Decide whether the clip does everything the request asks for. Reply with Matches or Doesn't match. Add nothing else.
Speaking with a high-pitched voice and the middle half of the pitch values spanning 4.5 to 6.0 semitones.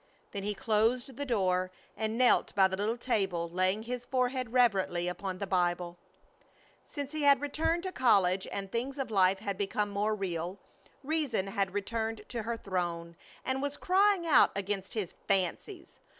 Matches